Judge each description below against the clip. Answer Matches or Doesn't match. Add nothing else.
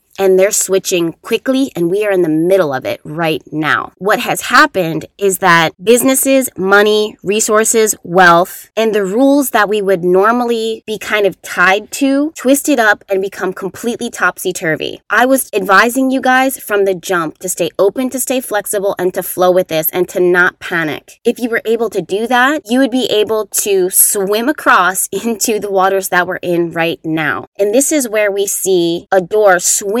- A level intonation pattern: Doesn't match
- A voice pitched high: Matches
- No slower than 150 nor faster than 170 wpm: Doesn't match